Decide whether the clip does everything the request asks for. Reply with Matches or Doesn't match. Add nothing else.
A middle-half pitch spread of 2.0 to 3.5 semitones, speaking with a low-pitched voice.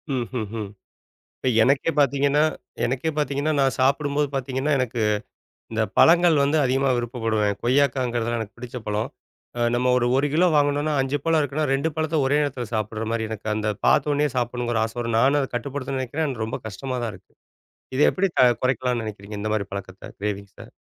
Doesn't match